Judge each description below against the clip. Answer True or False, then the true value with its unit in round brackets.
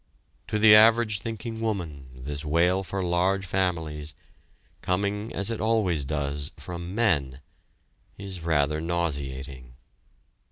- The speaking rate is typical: False (115 wpm)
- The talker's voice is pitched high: False (85 Hz)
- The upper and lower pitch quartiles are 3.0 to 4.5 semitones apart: False (5.6 semitones)